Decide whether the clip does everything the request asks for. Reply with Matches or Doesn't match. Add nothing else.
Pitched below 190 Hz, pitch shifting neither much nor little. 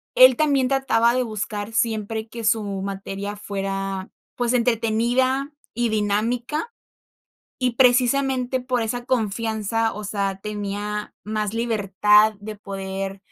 Doesn't match